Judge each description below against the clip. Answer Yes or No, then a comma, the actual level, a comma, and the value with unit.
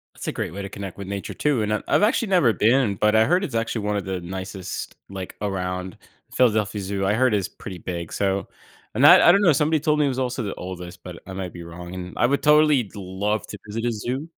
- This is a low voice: Yes, low, 105 Hz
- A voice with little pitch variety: No, average, 5.3 semitones